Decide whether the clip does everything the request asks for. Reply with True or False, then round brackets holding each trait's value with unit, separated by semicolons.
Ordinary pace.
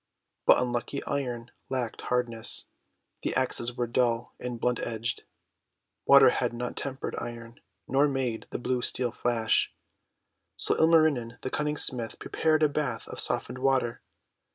True (145 wpm)